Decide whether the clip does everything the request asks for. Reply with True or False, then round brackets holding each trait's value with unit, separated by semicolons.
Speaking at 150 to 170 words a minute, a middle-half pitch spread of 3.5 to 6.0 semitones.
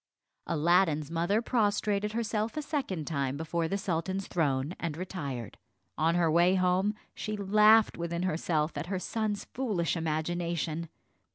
False (140 wpm; 4.2 semitones)